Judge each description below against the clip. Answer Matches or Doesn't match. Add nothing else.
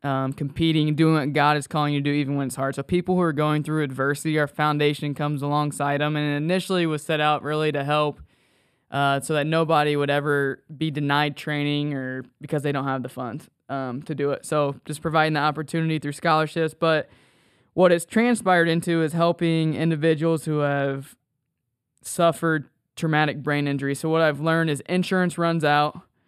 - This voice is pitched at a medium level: Matches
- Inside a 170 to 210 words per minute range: Matches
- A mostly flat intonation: Matches